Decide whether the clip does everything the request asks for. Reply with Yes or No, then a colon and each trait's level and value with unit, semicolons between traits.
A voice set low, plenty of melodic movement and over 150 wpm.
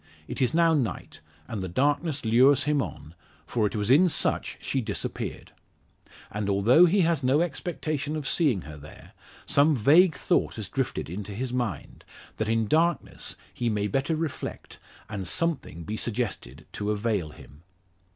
Yes: low, 125 Hz; wide, 6.8 semitones; average, 160 wpm